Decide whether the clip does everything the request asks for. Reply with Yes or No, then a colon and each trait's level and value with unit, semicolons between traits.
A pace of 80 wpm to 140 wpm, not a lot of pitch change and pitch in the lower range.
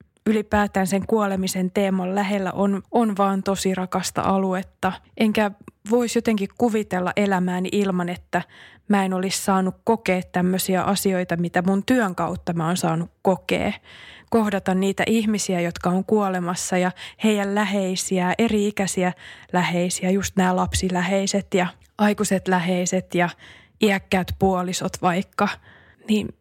No: average, 125 wpm; narrow, 1.9 semitones; high, 190 Hz